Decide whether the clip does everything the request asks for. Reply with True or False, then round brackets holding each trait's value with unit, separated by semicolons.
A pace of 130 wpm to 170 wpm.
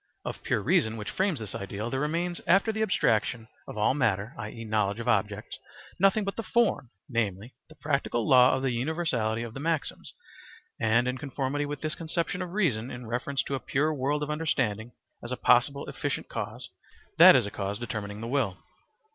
False (190 wpm)